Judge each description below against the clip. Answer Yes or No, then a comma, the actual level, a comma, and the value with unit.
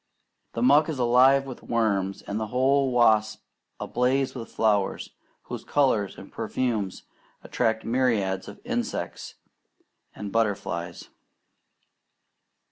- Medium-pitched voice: No, low, 115 Hz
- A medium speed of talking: No, slow, 110 wpm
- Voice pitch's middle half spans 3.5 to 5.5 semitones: Yes, average, 3.9 semitones